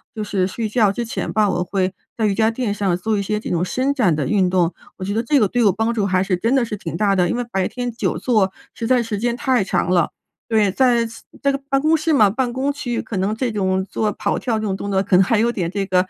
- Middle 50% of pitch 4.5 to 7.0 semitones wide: No, average, 3.9 semitones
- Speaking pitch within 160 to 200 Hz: No, high, 210 Hz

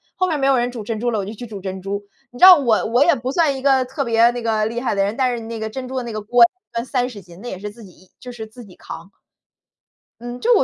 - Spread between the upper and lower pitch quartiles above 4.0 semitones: No, average, 3.2 semitones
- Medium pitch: No, high, 235 Hz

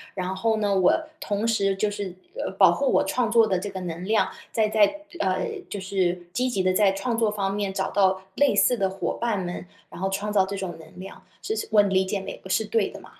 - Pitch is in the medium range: No, high, 200 Hz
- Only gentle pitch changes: Yes, narrow, 2.3 semitones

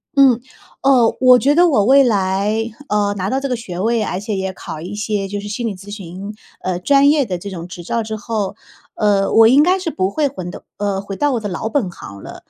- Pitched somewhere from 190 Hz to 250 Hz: Yes, high, 210 Hz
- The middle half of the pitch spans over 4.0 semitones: Yes, average, 4.6 semitones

